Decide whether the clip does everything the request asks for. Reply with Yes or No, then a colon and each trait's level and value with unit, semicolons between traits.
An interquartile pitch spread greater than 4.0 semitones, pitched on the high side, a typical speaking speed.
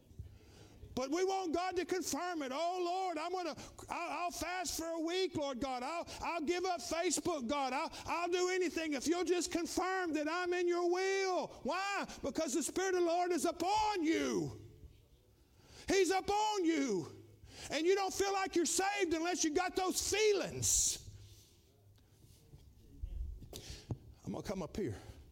Yes: average, 4.6 semitones; very high, 340 Hz; average, 160 wpm